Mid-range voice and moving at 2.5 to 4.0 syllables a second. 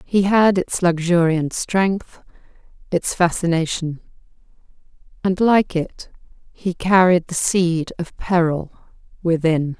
Yes: medium, 175 Hz; 3.6 syllables/s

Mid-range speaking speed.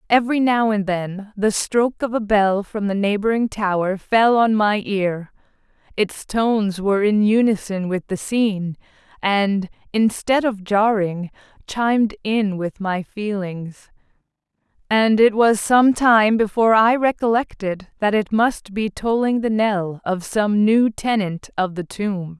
Yes: average, 150 wpm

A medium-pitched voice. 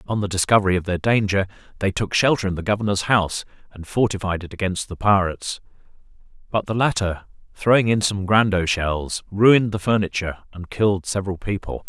No: low, 100 Hz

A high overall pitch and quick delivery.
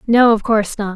Yes: high, 220 Hz; fast, 255 wpm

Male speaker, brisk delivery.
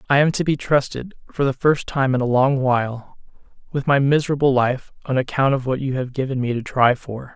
Yes: male; fast, 230 wpm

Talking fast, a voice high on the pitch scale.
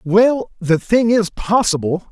No: average, 140 wpm; high, 200 Hz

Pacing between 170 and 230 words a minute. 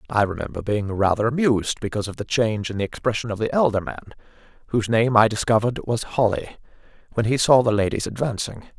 Yes: average, 190 wpm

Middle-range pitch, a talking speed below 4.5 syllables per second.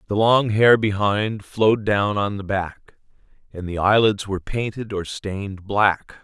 No: low, 100 Hz; 4.2 syllables/s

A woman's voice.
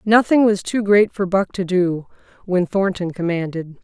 Yes: female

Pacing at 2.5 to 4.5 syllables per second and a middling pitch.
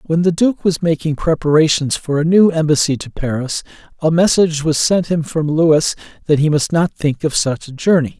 No: 5.1 syllables/s; medium, 155 Hz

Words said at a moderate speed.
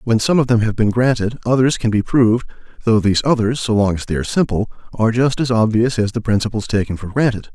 No: fast, 240 wpm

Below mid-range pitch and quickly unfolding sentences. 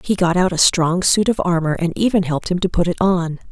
No: medium, 175 Hz; fast, 275 wpm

